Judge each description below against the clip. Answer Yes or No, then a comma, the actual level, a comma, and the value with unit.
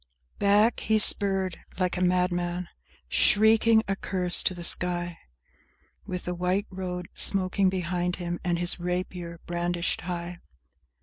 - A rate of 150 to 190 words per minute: No, slow, 135 wpm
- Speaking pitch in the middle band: Yes, medium, 180 Hz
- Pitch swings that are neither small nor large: No, narrow, 1.5 semitones